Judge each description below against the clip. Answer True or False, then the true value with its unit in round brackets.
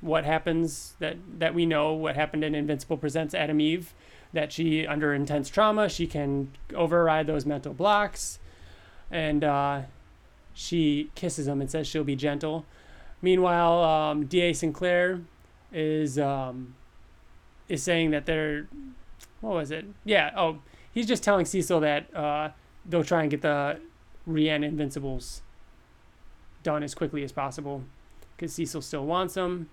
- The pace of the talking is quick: False (145 wpm)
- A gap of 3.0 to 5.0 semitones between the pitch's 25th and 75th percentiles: False (2.5 semitones)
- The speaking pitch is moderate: True (155 Hz)